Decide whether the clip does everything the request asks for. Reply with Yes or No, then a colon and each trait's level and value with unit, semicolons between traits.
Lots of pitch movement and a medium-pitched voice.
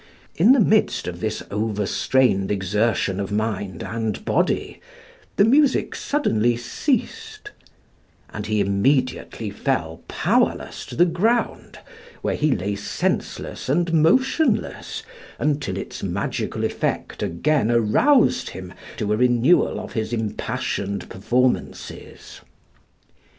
No: wide, 8.8 semitones; low, 120 Hz